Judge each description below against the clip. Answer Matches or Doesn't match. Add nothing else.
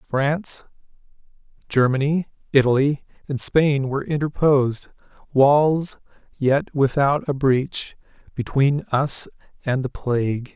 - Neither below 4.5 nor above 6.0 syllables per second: Doesn't match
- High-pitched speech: Doesn't match